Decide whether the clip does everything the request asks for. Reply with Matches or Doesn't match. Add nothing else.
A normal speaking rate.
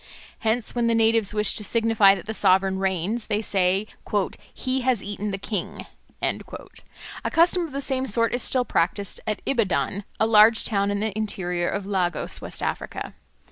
Matches